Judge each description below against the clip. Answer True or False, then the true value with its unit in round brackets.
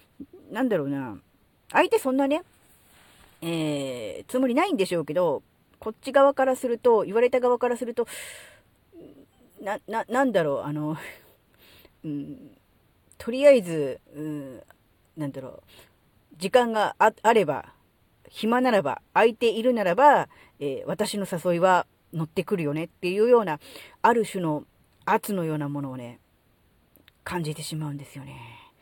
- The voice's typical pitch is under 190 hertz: False (195 Hz)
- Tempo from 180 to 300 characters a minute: True (275 characters per minute)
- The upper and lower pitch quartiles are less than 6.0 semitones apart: False (8.7 semitones)